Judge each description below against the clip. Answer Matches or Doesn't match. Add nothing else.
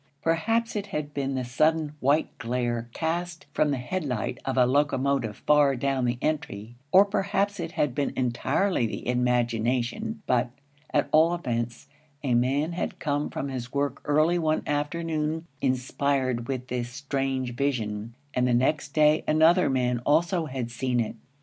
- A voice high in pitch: Doesn't match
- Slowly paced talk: Doesn't match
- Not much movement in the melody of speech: Doesn't match